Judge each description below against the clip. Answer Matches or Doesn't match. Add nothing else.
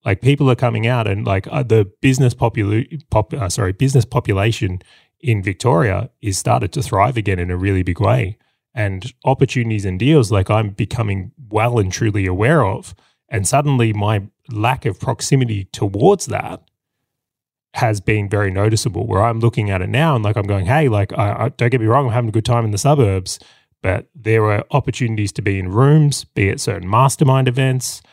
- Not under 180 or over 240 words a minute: Matches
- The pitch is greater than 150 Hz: Doesn't match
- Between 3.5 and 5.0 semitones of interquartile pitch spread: Matches